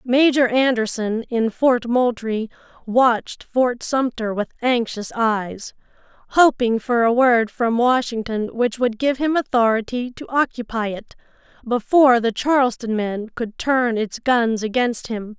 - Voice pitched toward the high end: Yes, high, 235 Hz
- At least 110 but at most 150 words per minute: Yes, slow, 135 wpm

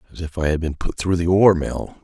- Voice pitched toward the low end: Yes, very low, 85 Hz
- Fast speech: Yes, fast, 295 wpm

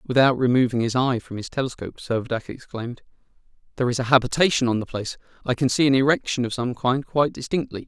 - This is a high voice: No, low, 125 Hz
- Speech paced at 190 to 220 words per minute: Yes, average, 200 wpm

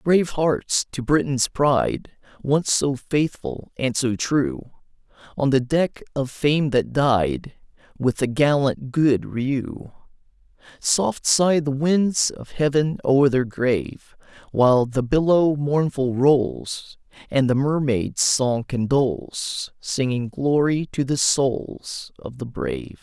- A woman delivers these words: No, male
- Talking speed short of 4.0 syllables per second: Yes, 3.4 syllables/s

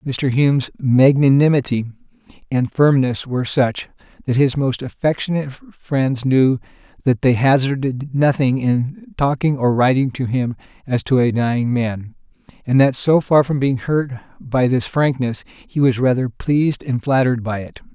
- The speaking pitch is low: Yes, low, 130 Hz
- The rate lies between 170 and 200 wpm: No, average, 155 wpm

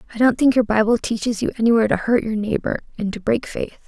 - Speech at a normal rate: No, fast, 250 wpm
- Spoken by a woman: Yes, female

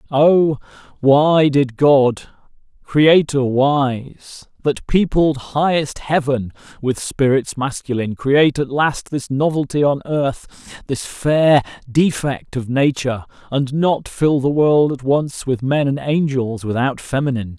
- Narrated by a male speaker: Yes, male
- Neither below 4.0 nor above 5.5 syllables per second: No, 3.7 syllables/s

